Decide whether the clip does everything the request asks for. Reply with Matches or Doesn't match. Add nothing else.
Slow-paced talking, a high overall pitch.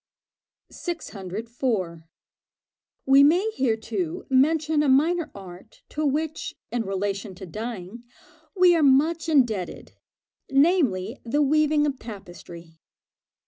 Matches